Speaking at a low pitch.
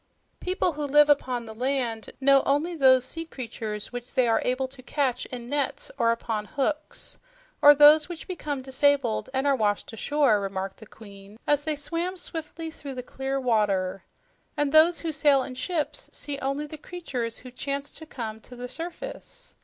No: very high, 270 Hz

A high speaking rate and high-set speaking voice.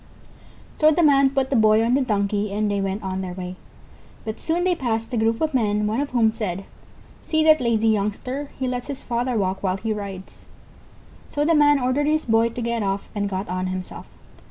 Yes: fast, 215 wpm; high, 225 Hz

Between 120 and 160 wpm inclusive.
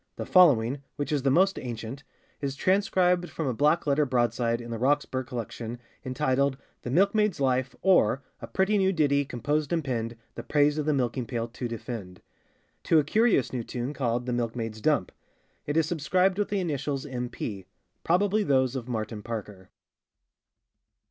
No: average, 175 wpm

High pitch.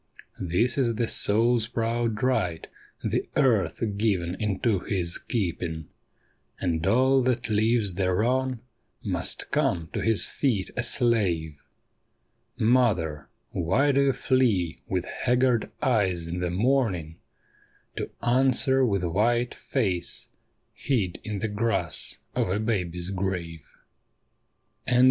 No: low, 105 Hz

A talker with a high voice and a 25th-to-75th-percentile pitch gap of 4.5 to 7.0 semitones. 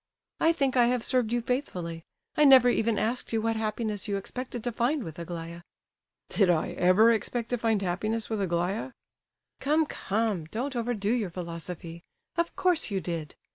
Yes: high, 220 Hz; wide, 5.4 semitones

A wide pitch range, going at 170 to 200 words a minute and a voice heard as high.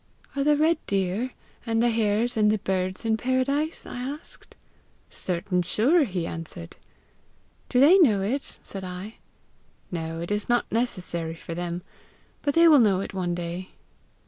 No: wide, 6.2 semitones; average, 160 wpm; high, 210 Hz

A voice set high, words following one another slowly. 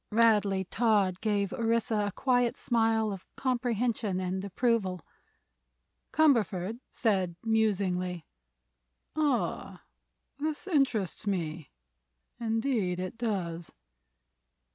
Yes: high, 215 Hz; slow, 85 wpm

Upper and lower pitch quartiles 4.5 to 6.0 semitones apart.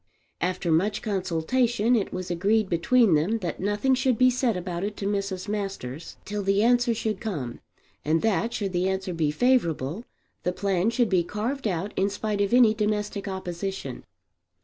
No: average, 3.7 semitones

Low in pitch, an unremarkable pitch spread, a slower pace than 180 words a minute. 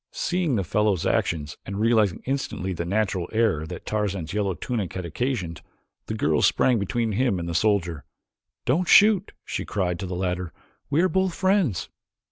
No: low, 100 Hz; wide, 5.8 semitones; average, 170 wpm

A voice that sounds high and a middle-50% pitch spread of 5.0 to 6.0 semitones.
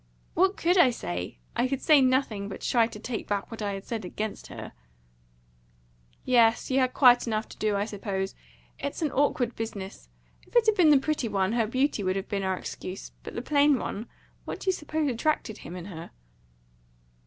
Yes: high, 230 Hz; wide, 5.6 semitones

